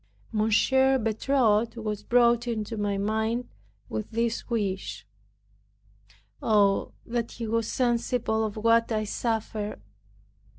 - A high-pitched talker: Yes, high, 225 Hz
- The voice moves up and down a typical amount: No, narrow, 1.8 semitones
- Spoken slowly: Yes, slow, 110 wpm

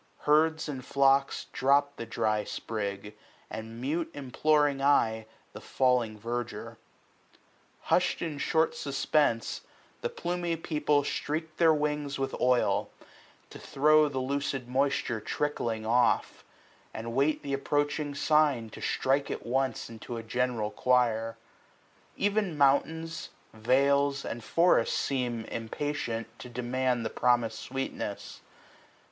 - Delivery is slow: Yes, slow, 125 wpm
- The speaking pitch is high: No, low, 135 Hz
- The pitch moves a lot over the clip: No, average, 4.0 semitones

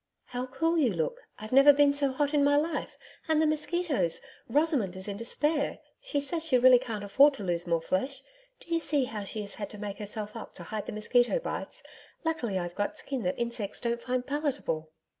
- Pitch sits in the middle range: No, very high, 255 Hz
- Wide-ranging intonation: Yes, wide, 6.0 semitones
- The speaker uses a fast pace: Yes, fast, 215 wpm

